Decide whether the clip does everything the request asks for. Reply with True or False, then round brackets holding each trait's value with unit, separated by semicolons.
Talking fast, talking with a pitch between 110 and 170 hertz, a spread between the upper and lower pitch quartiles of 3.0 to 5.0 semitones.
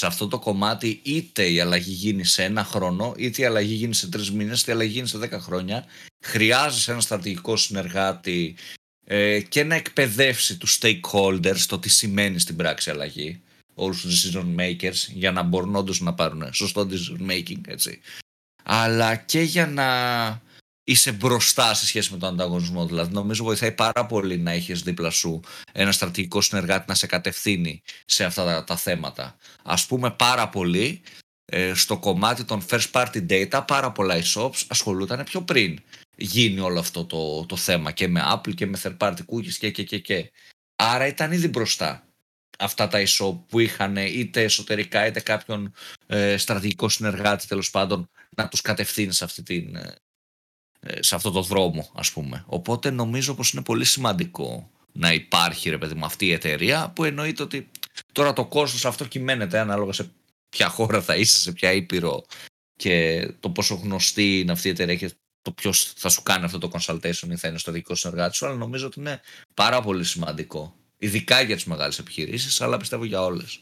False (180 wpm; 100 Hz; 4.4 semitones)